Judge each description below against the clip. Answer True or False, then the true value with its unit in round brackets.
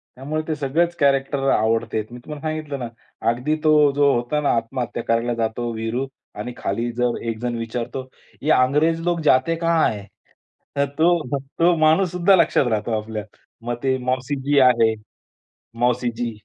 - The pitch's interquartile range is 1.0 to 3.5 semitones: False (4.5 semitones)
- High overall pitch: False (130 Hz)